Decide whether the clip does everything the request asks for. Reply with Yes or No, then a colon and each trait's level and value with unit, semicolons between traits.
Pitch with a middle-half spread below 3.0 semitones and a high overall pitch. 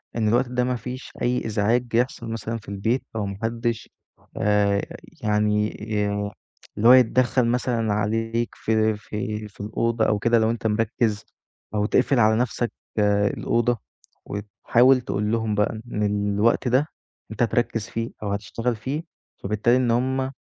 No: narrow, 2.4 semitones; low, 115 Hz